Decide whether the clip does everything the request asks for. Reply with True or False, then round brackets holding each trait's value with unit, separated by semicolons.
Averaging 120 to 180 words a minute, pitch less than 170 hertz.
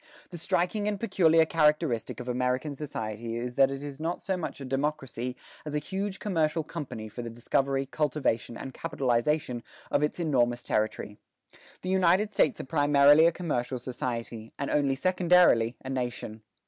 True (160 wpm; 140 Hz)